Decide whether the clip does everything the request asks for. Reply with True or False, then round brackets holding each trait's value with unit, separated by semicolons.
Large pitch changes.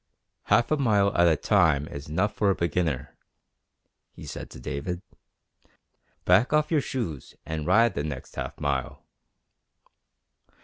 True (6.2 semitones)